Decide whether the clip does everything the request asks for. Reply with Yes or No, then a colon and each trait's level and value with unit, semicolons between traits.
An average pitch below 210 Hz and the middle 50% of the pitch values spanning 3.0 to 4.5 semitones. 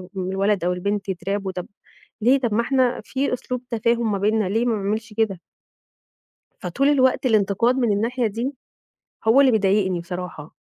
No: high, 215 Hz; average, 3.9 semitones